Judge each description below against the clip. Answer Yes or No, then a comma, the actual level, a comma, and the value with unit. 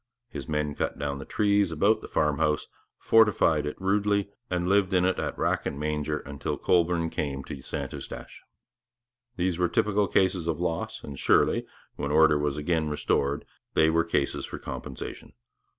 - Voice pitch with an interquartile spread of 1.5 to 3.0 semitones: No, average, 4.0 semitones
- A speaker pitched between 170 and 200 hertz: No, very low, 80 Hz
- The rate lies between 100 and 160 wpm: No, average, 170 wpm